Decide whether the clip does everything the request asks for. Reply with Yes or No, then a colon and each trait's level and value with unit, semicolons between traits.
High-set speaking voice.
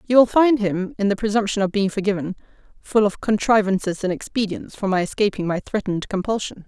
Yes: high, 205 Hz